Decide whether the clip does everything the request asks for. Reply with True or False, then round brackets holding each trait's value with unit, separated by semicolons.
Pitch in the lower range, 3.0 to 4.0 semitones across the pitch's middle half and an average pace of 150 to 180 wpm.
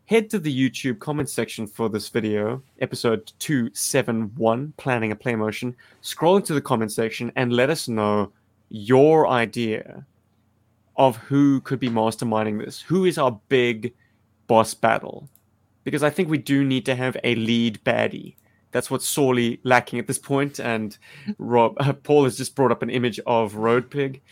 True (120 Hz; 3.5 semitones; 170 wpm)